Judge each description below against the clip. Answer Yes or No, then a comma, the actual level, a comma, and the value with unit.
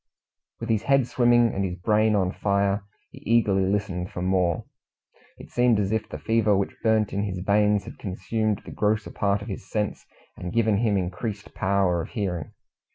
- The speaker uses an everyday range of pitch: No, narrow, 2.3 semitones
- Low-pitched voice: Yes, low, 100 Hz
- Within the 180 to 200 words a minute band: Yes, average, 185 wpm